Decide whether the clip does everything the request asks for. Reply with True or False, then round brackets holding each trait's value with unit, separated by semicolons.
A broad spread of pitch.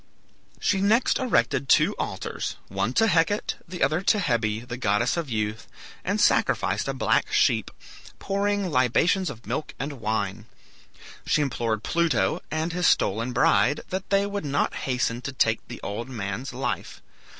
True (7.7 semitones)